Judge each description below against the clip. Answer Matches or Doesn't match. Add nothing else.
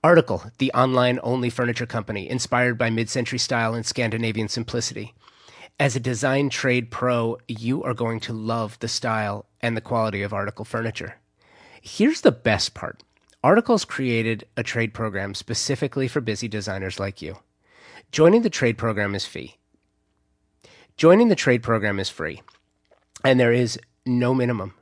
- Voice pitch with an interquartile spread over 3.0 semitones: Doesn't match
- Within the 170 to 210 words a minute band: Doesn't match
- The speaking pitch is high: Doesn't match